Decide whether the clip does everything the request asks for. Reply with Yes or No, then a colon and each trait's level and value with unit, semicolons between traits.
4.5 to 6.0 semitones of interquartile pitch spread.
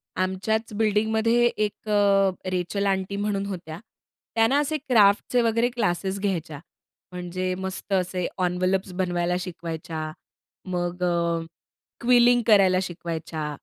No: average, 3.3 semitones